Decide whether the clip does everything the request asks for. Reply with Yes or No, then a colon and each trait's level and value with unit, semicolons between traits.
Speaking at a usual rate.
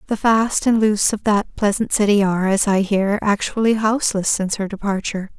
Yes: average, 190 wpm